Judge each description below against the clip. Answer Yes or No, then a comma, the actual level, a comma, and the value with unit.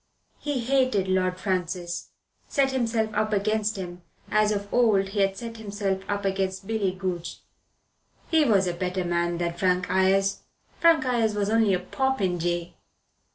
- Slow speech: No, average, 155 wpm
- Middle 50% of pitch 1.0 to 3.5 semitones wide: Yes, average, 3.1 semitones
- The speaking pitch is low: No, high, 195 Hz